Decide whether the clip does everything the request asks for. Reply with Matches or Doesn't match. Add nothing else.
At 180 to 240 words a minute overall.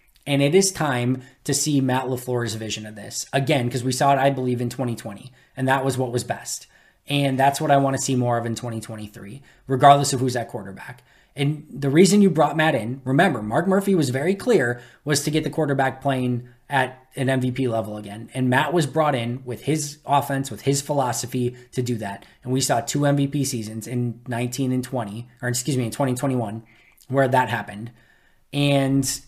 Matches